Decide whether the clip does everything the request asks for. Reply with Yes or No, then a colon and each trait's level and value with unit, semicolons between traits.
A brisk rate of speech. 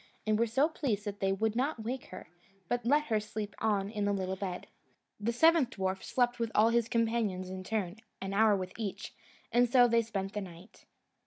Yes: fast, 210 wpm